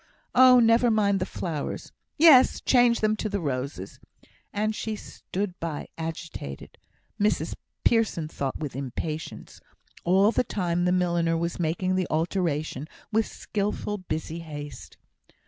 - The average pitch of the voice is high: No, medium, 180 Hz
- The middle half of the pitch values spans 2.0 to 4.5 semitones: No, average, 5.2 semitones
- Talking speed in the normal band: No, slow, 130 wpm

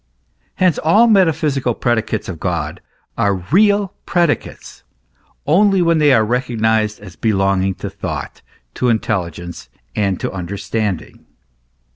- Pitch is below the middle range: Yes, low, 110 Hz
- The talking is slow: Yes, slow, 125 wpm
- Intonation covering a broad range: Yes, wide, 8.6 semitones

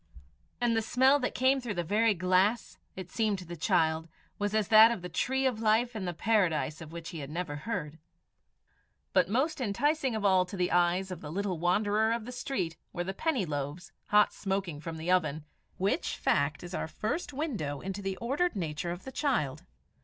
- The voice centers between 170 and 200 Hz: Yes, high, 190 Hz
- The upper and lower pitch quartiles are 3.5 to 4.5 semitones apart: No, average, 5.2 semitones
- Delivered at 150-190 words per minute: No, fast, 205 wpm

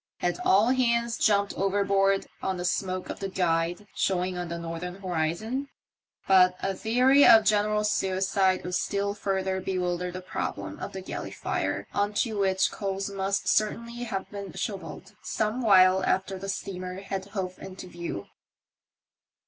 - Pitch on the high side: Yes, high, 195 Hz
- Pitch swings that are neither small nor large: No, narrow, 2.1 semitones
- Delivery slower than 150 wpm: No, average, 155 wpm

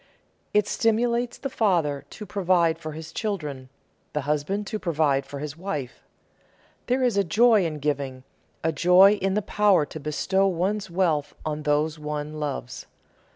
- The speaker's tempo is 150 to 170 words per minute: Yes, average, 155 wpm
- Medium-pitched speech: Yes, medium, 165 Hz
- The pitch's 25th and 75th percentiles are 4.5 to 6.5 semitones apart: Yes, average, 5.2 semitones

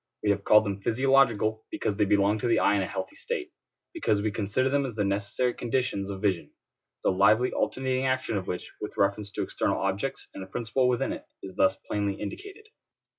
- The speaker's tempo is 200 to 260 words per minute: Yes, fast, 205 wpm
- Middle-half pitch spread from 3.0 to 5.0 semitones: Yes, average, 4.5 semitones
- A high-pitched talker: No, low, 105 Hz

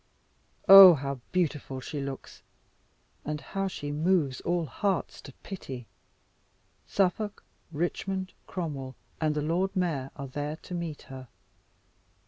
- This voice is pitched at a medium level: Yes, medium, 155 Hz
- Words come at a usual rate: No, slow, 120 wpm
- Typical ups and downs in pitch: Yes, average, 4.9 semitones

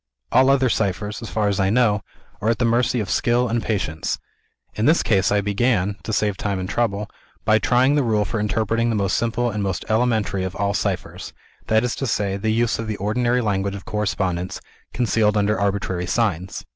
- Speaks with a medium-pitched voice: No, low, 105 Hz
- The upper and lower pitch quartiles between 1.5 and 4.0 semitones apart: Yes, average, 2.8 semitones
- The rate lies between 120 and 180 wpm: No, fast, 205 wpm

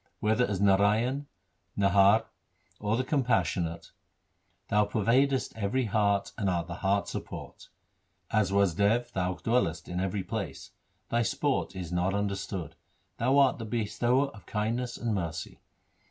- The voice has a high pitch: No, low, 105 Hz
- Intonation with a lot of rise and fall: No, average, 3.6 semitones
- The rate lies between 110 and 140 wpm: Yes, slow, 135 wpm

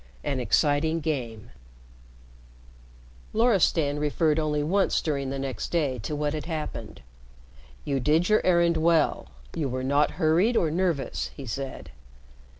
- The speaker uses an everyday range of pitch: Yes, average, 3.1 semitones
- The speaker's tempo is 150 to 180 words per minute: No, average, 140 wpm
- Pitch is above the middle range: No, medium, 150 Hz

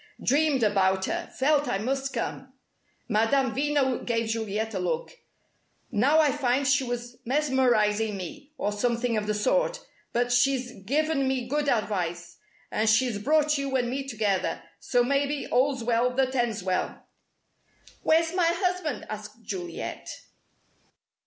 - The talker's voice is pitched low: No, high, 245 Hz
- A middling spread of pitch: Yes, average, 4.5 semitones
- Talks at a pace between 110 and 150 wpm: Yes, average, 140 wpm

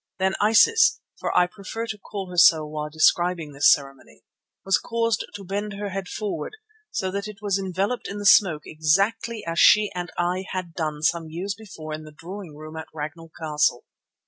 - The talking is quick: No, average, 190 wpm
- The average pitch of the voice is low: No, medium, 185 Hz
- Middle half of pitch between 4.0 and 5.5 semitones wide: Yes, average, 4.4 semitones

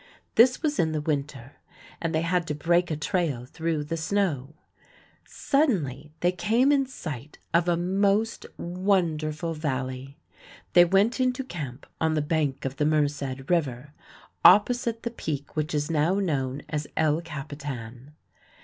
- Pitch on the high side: No, medium, 155 Hz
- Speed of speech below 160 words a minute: Yes, average, 150 wpm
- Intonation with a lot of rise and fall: No, average, 4.1 semitones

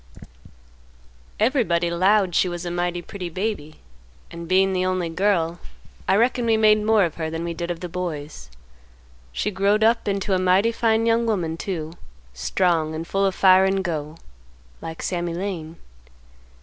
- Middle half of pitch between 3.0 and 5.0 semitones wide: Yes, average, 3.3 semitones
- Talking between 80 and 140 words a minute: No, average, 165 wpm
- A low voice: No, medium, 185 Hz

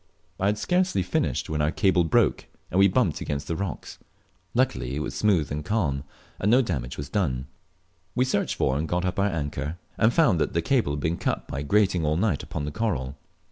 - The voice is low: Yes, very low, 85 Hz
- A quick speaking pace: Yes, fast, 215 wpm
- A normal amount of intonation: No, wide, 6.0 semitones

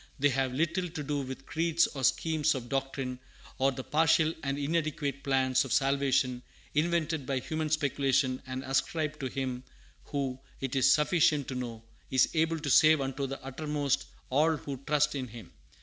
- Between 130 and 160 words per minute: No, average, 170 wpm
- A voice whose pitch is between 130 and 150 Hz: Yes, medium, 140 Hz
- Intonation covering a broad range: No, average, 2.7 semitones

